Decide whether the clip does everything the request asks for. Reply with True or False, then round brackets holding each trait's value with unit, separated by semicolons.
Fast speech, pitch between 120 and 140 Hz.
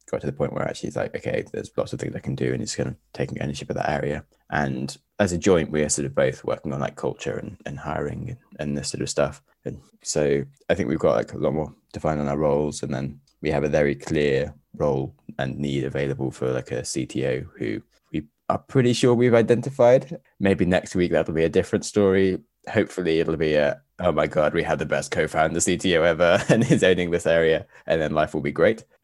False (245 wpm; 80 Hz)